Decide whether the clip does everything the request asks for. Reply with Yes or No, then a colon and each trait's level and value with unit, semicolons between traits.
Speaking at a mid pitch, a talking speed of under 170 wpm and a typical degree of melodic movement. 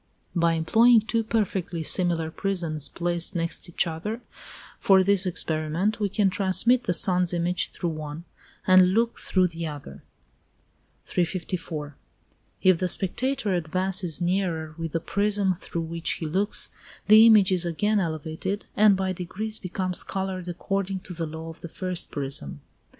Yes: medium, 180 Hz; average, 150 wpm; average, 3.0 semitones